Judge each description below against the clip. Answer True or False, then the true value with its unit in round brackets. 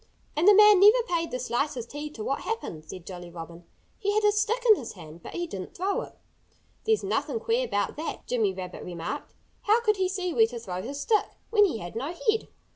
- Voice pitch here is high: True (300 Hz)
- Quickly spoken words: True (225 wpm)